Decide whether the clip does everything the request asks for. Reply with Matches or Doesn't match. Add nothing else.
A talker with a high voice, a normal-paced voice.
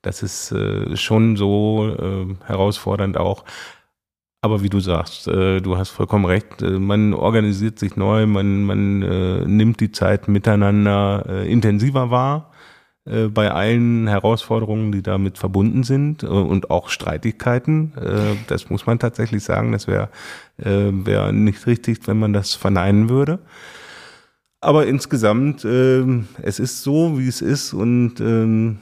Doesn't match